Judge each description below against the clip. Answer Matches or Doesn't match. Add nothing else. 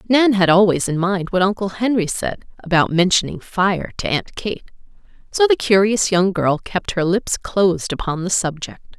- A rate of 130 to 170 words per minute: Doesn't match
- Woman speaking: Matches